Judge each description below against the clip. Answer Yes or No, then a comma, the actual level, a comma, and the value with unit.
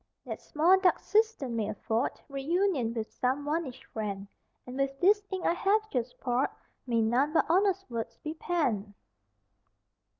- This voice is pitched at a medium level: No, very high, 275 Hz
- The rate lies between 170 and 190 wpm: No, average, 155 wpm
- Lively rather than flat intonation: Yes, wide, 7.2 semitones